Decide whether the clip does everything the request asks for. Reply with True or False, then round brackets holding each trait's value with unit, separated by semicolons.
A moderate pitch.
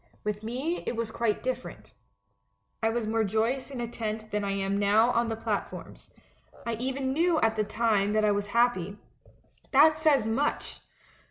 False (225 Hz)